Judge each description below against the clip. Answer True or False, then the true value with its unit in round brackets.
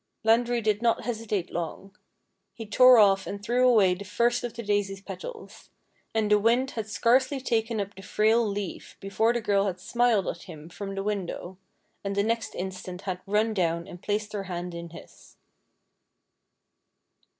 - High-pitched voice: True (210 Hz)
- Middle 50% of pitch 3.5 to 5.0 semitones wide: False (3.1 semitones)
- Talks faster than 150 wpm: True (170 wpm)